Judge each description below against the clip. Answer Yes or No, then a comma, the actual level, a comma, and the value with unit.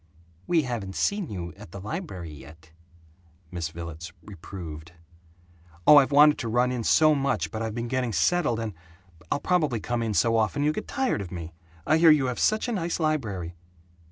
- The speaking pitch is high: No, low, 115 Hz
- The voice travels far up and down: Yes, wide, 8.8 semitones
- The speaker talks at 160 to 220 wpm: Yes, average, 185 wpm